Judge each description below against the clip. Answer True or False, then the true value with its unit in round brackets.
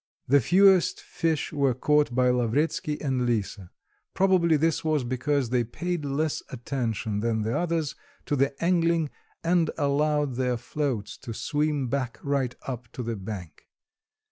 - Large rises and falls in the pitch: False (4.3 semitones)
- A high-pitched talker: False (140 Hz)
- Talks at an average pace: True (145 wpm)